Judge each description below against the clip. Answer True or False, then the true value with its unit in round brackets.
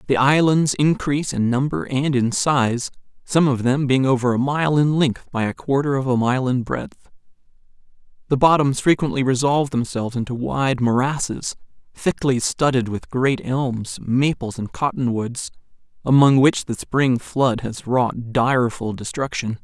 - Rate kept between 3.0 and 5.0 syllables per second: True (4.5 syllables/s)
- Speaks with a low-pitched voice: True (130 Hz)